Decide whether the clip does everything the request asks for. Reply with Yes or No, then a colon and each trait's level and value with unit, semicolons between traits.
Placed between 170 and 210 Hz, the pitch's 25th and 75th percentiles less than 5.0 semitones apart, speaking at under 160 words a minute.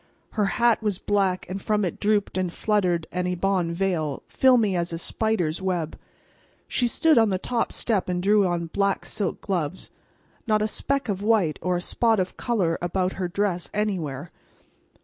No: high, 190 Hz; average, 3.3 semitones; average, 175 wpm